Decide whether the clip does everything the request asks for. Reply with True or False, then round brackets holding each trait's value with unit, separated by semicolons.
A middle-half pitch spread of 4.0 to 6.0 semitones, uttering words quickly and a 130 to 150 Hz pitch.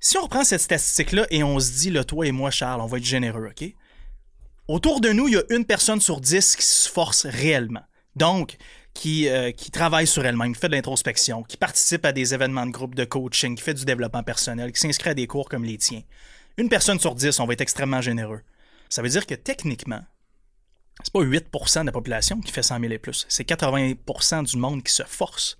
True (5.3 semitones; 230 wpm; 135 Hz)